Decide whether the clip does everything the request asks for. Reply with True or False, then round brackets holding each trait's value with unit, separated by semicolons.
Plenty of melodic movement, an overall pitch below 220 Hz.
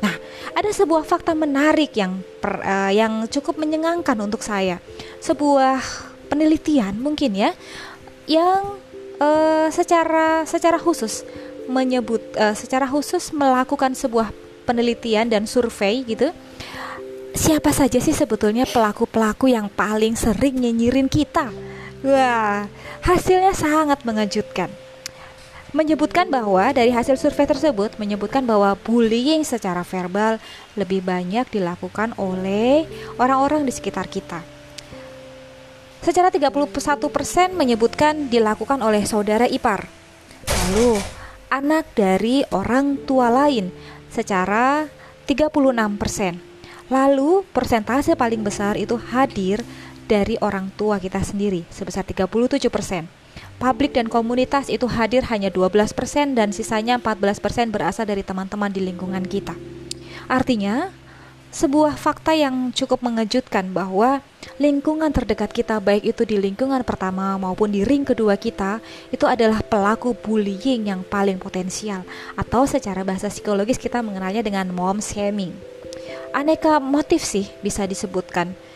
False (5.7 semitones; 230 Hz)